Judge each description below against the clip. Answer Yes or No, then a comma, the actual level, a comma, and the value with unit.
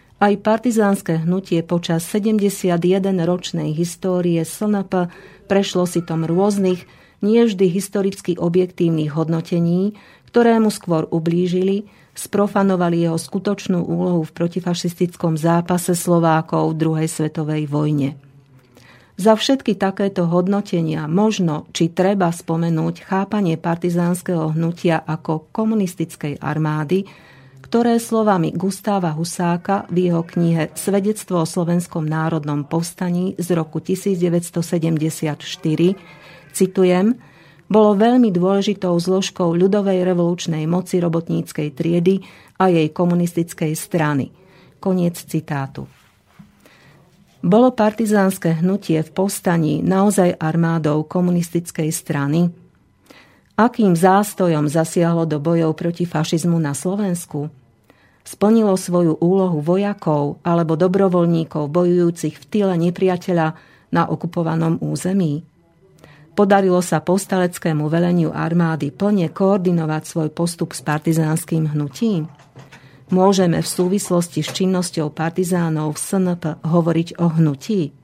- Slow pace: Yes, slow, 100 wpm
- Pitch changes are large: No, average, 2.9 semitones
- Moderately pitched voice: Yes, medium, 175 Hz